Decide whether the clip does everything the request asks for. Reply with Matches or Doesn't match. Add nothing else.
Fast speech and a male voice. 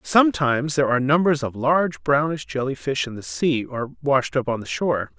Matches